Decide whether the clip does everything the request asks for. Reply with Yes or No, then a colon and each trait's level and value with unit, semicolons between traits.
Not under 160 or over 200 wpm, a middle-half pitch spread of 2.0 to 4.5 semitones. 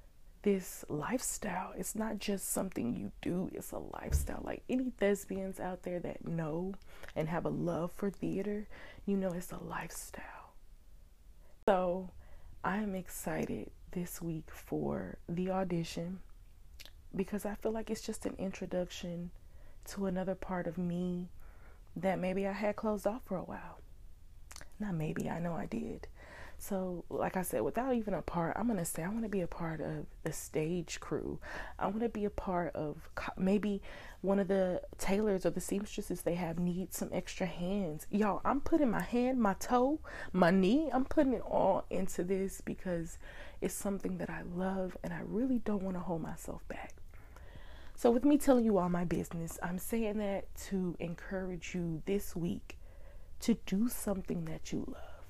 Yes: average, 175 wpm; average, 3.3 semitones